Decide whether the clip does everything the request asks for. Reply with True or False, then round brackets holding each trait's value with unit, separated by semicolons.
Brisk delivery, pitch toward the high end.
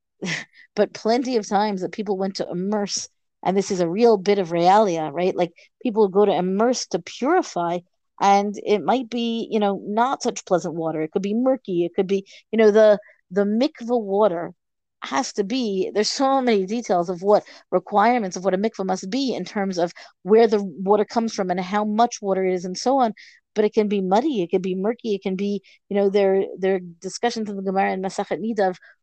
True (215 wpm; 200 Hz)